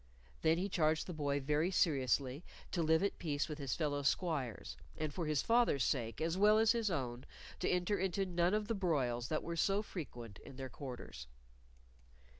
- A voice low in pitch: No, medium, 155 Hz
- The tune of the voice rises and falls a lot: No, average, 5.0 semitones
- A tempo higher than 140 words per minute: Yes, average, 190 wpm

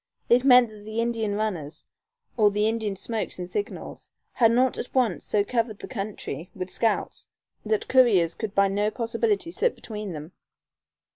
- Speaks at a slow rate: No, average, 165 wpm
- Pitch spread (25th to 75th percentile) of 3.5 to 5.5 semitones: No, average, 2.9 semitones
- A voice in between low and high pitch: No, high, 215 Hz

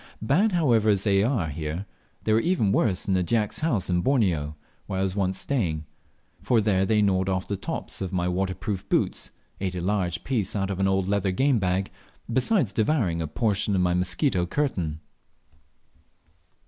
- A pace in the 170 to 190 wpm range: Yes, average, 180 wpm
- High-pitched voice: No, very low, 95 Hz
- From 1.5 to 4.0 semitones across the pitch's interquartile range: Yes, average, 3.4 semitones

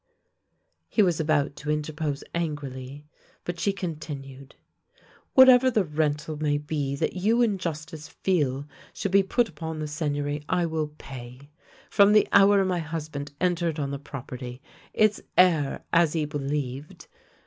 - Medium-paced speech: Yes, average, 160 wpm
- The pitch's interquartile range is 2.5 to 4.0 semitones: Yes, average, 3.7 semitones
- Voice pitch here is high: No, medium, 155 Hz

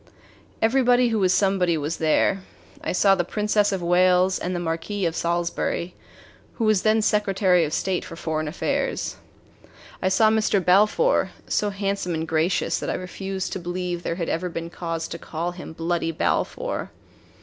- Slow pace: No, average, 170 wpm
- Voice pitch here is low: No, medium, 180 Hz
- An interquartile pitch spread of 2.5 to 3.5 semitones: Yes, average, 3.1 semitones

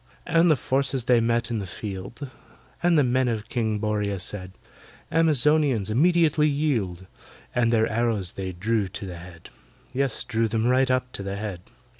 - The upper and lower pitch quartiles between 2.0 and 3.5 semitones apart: No, average, 4.8 semitones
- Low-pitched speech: Yes, low, 115 Hz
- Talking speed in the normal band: Yes, average, 170 wpm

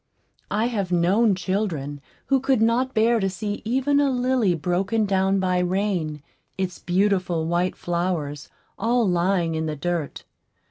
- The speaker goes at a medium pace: Yes, average, 145 wpm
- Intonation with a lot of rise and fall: No, average, 4.4 semitones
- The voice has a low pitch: No, high, 190 Hz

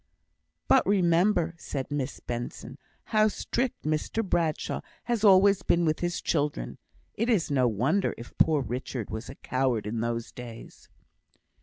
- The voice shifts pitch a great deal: Yes, wide, 7.5 semitones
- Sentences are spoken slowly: No, average, 145 wpm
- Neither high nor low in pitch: Yes, medium, 150 Hz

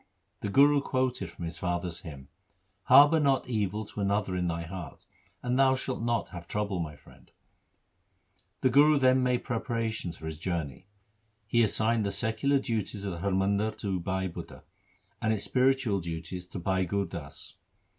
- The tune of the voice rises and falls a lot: Yes, wide, 5.7 semitones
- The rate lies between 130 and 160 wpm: No, average, 180 wpm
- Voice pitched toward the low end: Yes, low, 100 Hz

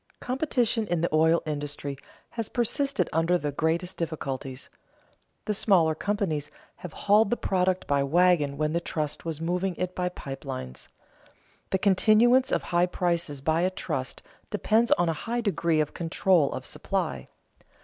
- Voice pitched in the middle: Yes, medium, 175 Hz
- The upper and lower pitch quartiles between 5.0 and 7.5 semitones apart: No, average, 4.4 semitones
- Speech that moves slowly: No, average, 155 wpm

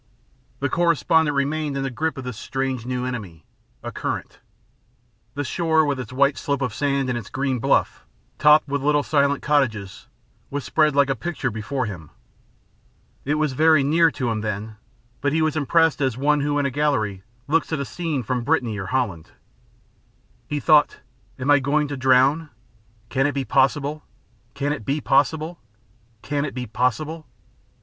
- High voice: No, medium, 140 Hz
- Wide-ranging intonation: No, average, 2.9 semitones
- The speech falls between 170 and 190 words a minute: Yes, average, 175 wpm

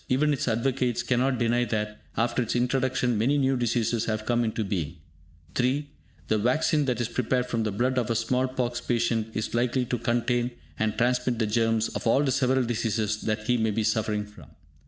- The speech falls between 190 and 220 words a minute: Yes, average, 200 wpm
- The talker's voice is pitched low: Yes, low, 120 Hz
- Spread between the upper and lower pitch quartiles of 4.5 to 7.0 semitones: No, narrow, 2.4 semitones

